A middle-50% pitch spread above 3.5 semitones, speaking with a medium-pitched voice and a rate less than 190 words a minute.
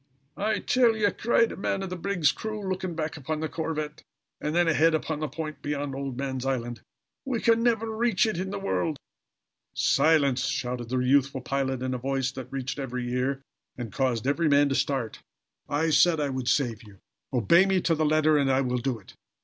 No: average, 4.7 semitones; medium, 145 Hz; fast, 205 wpm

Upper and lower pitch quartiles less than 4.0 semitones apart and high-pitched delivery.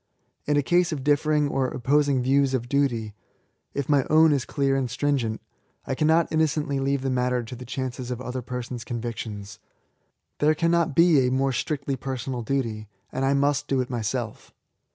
No: average, 2.7 semitones; low, 135 Hz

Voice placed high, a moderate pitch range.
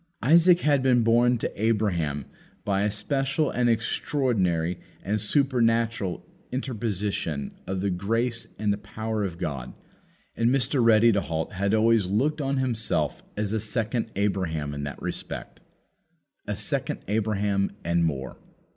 No: low, 110 Hz; average, 3.8 semitones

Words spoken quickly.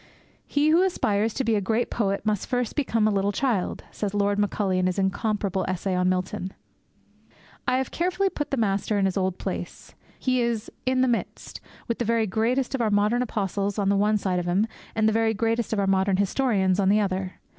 Yes: fast, 215 wpm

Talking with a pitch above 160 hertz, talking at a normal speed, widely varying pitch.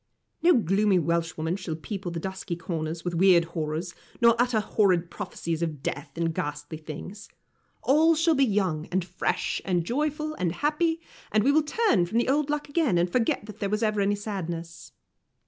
Yes: high, 190 Hz; average, 180 wpm; wide, 6.5 semitones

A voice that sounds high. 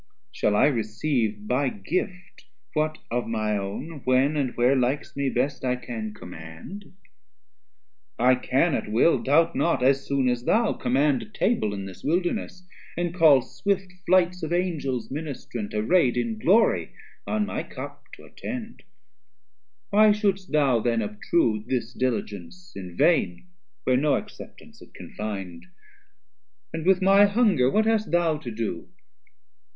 No: low, 135 Hz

